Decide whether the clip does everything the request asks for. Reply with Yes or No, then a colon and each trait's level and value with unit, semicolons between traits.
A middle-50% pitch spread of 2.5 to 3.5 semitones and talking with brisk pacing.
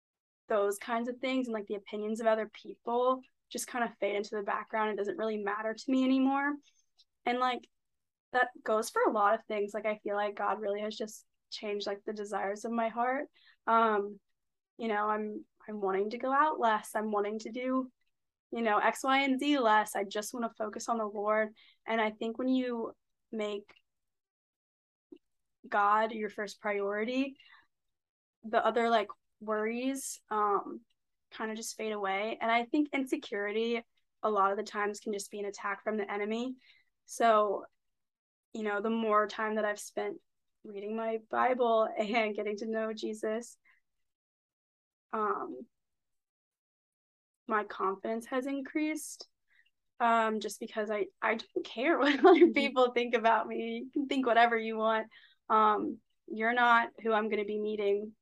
No: average, 2.9 semitones; average, 170 wpm